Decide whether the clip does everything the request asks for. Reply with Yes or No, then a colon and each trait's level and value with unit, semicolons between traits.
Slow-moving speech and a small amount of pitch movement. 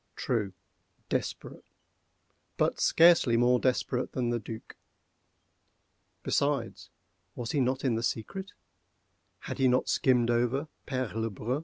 Yes: slow, 115 wpm; narrow, 2.3 semitones